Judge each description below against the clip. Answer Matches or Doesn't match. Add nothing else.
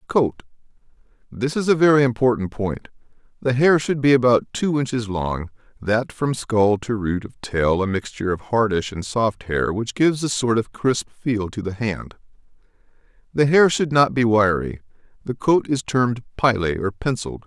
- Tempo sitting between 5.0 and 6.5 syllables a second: Doesn't match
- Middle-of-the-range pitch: Doesn't match